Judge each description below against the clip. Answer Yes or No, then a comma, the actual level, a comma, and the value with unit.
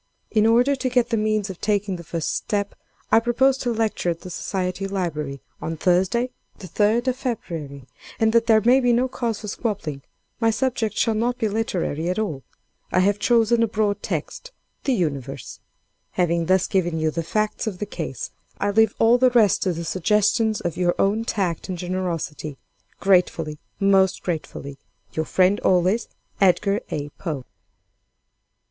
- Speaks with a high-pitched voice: Yes, high, 200 Hz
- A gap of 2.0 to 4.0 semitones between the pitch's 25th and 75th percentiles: No, average, 4.6 semitones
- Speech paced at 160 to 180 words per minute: Yes, average, 170 wpm